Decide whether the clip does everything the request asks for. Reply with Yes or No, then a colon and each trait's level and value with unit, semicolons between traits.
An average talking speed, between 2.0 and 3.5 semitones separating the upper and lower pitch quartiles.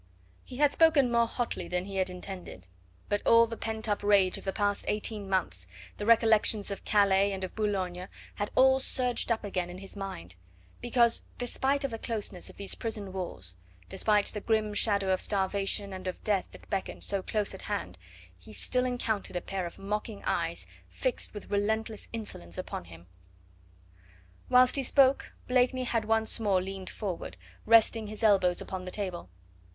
Yes: average, 175 wpm; average, 3.2 semitones